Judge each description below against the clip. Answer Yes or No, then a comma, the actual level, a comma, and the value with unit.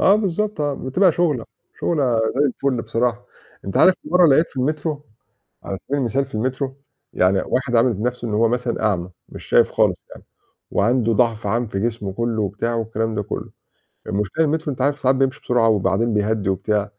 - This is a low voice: Yes, low, 120 Hz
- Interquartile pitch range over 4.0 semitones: Yes, average, 4.5 semitones